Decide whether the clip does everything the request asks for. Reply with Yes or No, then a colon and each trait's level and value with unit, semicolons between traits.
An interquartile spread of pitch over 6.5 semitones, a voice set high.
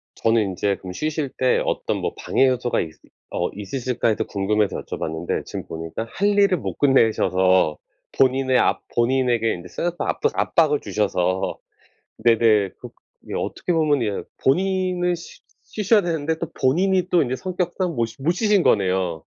No: wide, 8.8 semitones; low, 130 Hz